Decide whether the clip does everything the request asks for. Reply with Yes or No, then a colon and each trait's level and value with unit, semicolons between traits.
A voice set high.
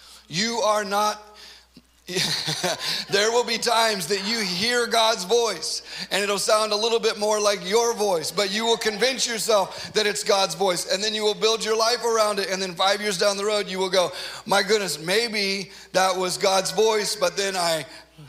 Yes: high, 210 Hz